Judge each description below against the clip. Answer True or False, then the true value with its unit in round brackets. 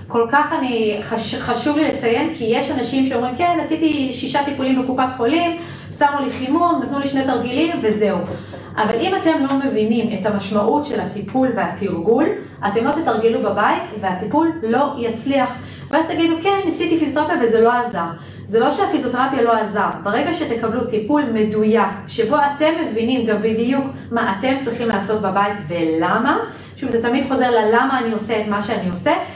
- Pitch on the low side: False (245 Hz)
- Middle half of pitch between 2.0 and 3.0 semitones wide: False (4.8 semitones)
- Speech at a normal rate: True (165 wpm)